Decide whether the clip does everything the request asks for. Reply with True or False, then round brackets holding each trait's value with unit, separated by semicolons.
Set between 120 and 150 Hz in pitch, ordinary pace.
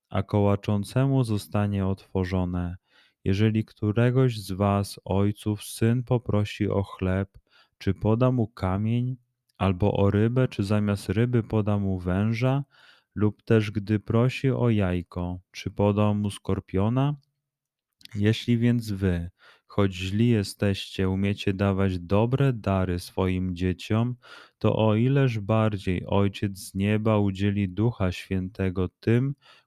False (105 Hz; 120 wpm)